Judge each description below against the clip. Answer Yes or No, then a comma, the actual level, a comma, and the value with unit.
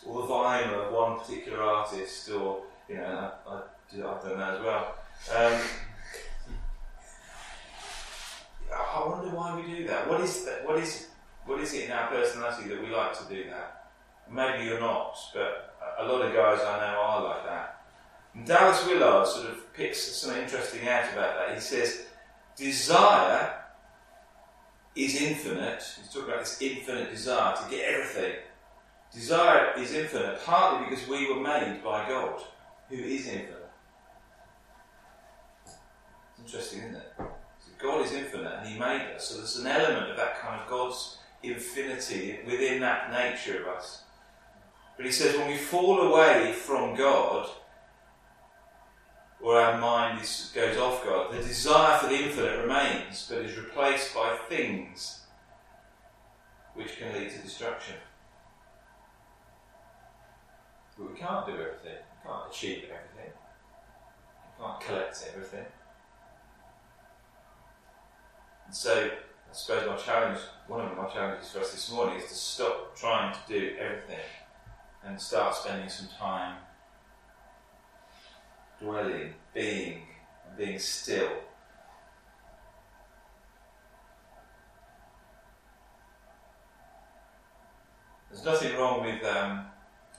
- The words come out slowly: Yes, slow, 130 wpm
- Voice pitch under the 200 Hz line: Yes, low, 135 Hz